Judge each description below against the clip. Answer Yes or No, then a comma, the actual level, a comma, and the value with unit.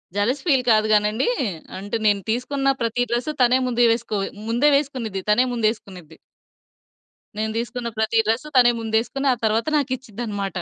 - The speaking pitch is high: Yes, high, 230 Hz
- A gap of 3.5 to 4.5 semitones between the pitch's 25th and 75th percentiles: No, average, 2.7 semitones